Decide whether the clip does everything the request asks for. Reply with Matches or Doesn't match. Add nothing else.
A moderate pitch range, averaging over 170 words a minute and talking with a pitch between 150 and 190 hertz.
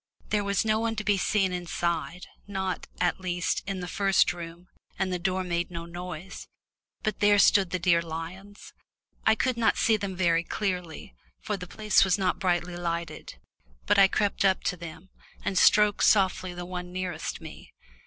Doesn't match